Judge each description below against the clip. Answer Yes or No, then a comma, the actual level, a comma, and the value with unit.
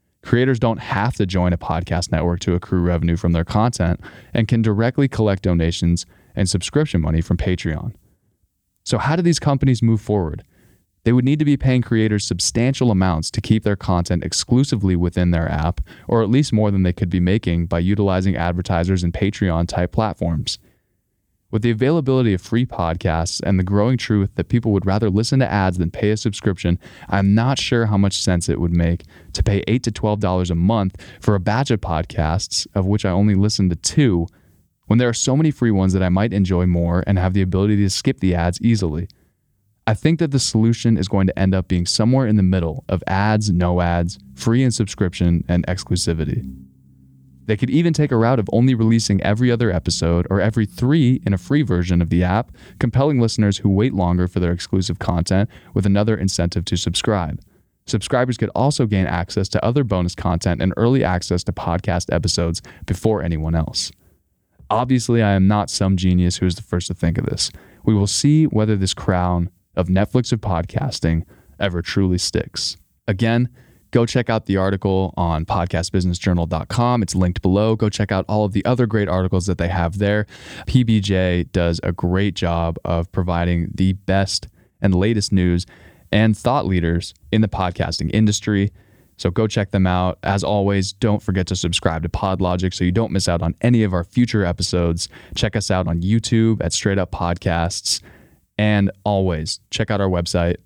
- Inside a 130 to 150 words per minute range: No, average, 190 wpm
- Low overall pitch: Yes, very low, 95 Hz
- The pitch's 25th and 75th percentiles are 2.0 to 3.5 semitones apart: No, average, 4.1 semitones